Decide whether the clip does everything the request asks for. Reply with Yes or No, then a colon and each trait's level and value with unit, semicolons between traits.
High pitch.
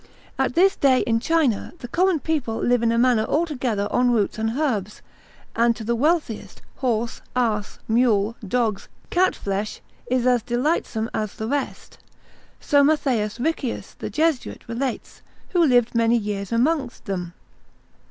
Yes: high, 240 Hz